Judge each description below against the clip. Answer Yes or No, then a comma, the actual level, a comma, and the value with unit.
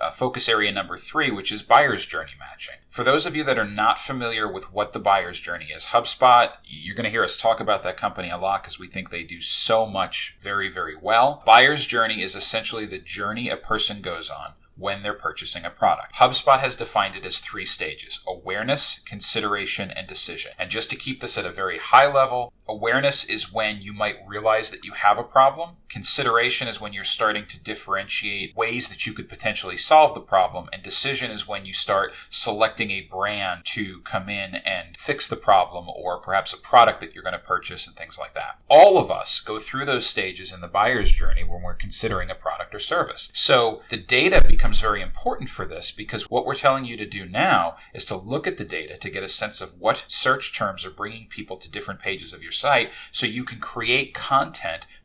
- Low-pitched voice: Yes, low, 105 Hz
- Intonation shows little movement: No, average, 3.9 semitones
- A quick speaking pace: Yes, fast, 215 wpm